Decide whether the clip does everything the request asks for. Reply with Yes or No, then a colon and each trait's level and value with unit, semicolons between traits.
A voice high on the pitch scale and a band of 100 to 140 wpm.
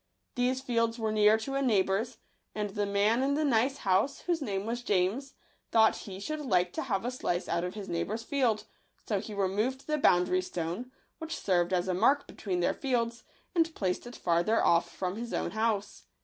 No: high, 220 Hz; fast, 205 wpm